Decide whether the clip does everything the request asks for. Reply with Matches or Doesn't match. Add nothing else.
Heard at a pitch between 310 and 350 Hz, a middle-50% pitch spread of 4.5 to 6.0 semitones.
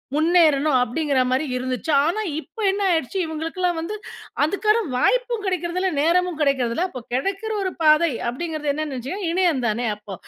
Matches